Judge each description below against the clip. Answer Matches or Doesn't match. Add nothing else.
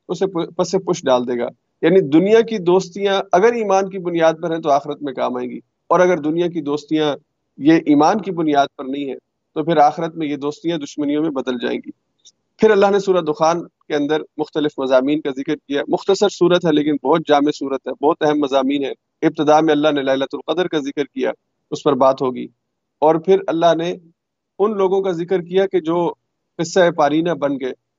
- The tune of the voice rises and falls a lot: Doesn't match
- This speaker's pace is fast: Matches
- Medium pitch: Matches